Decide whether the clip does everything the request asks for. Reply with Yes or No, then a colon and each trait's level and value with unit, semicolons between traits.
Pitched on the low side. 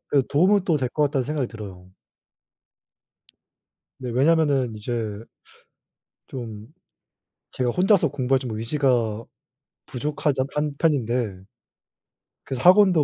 Yes: low, 130 Hz